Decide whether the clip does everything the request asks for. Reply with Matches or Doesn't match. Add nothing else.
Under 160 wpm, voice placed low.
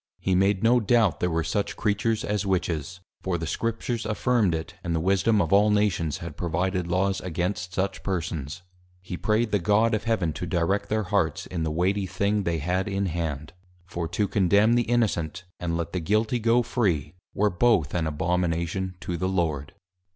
Doesn't match